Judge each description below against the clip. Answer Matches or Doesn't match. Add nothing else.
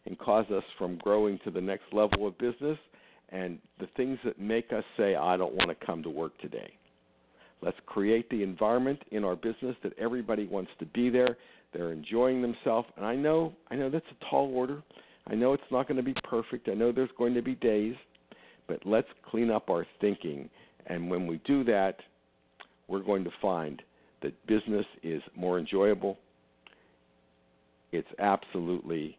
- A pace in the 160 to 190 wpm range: Matches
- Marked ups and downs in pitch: Matches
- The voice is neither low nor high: Doesn't match